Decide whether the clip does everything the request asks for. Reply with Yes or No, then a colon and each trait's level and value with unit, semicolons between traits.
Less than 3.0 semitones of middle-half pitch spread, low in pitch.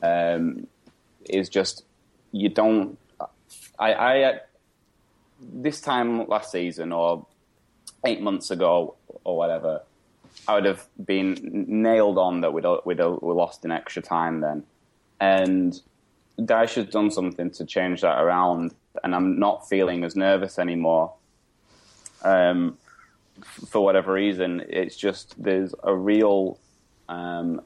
Yes: narrow, 2.4 semitones; very low, 95 Hz